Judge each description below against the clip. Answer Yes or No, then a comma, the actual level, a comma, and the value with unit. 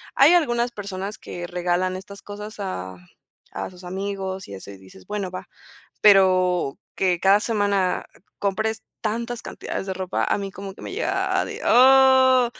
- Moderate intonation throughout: Yes, average, 3.1 semitones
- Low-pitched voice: No, high, 195 Hz